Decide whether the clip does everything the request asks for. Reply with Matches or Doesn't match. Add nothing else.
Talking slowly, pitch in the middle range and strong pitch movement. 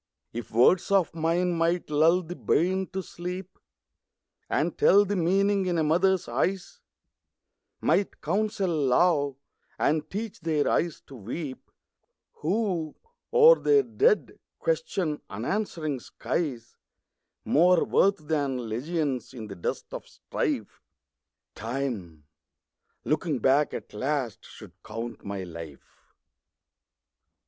Matches